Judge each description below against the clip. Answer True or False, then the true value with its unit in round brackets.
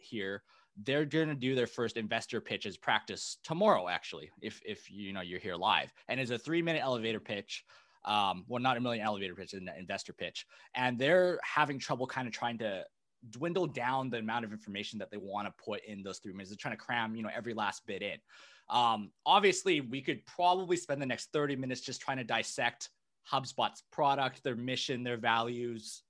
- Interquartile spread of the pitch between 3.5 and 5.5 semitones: True (4.0 semitones)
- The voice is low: True (125 Hz)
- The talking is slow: False (200 wpm)